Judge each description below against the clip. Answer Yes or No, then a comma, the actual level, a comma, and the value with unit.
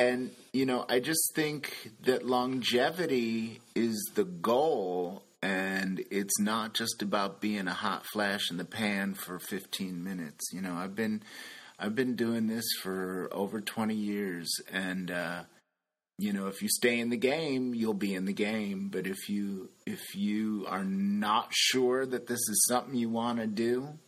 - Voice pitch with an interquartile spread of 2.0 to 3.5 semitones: No, average, 4.0 semitones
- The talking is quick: No, average, 170 wpm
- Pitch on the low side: Yes, low, 110 Hz